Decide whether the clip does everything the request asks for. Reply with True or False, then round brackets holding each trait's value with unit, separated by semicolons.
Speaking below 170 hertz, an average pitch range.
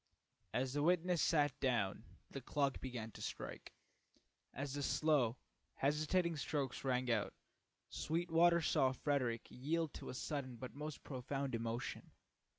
True (140 Hz; 3.5 semitones)